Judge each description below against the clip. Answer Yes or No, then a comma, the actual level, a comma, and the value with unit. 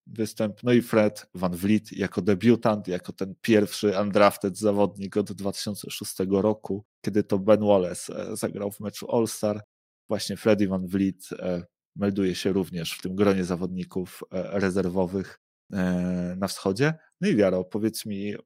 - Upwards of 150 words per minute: No, average, 140 wpm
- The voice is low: Yes, low, 100 Hz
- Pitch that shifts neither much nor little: No, narrow, 2.2 semitones